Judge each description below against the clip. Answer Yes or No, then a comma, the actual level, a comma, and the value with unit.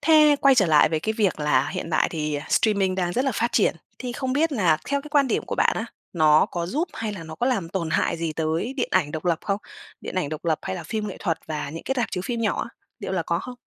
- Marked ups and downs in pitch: Yes, wide, 7.1 semitones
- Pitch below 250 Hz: Yes, medium, 185 Hz